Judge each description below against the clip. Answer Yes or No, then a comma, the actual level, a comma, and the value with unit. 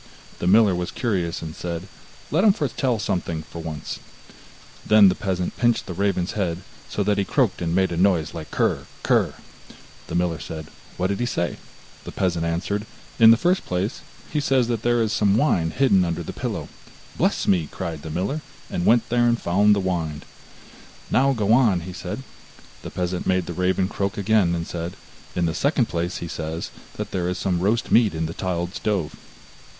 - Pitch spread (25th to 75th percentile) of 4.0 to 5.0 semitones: Yes, average, 4.3 semitones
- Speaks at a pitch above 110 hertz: No, very low, 95 Hz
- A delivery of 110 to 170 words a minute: No, average, 195 wpm